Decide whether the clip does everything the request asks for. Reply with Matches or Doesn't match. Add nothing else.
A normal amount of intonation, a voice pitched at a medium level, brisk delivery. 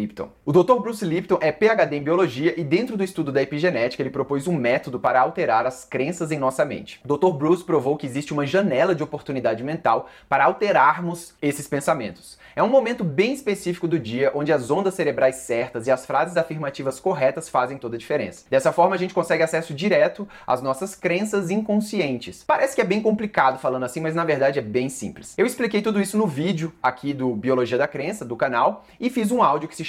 Doesn't match